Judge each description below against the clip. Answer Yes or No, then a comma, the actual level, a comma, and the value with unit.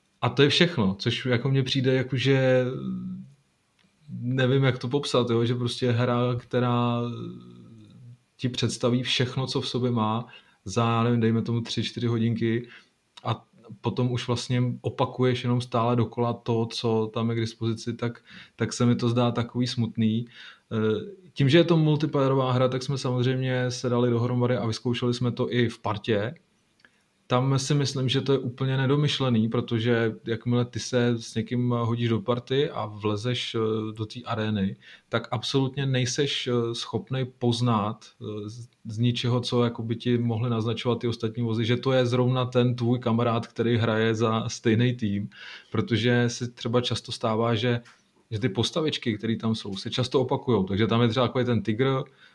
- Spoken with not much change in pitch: Yes, narrow, 1.7 semitones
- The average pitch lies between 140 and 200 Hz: No, low, 120 Hz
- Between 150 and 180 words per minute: Yes, average, 165 wpm